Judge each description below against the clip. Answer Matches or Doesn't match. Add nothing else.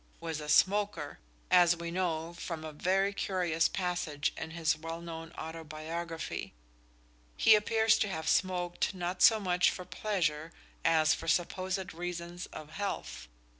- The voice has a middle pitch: Matches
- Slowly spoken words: Doesn't match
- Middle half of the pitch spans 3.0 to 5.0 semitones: Doesn't match